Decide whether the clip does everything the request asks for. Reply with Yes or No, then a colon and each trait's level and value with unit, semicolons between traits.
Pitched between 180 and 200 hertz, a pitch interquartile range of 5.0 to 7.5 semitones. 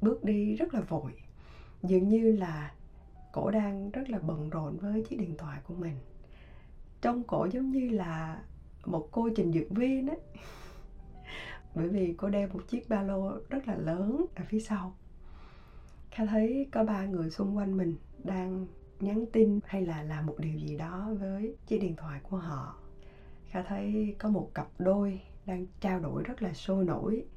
Yes: high, 190 Hz; wide, 5.5 semitones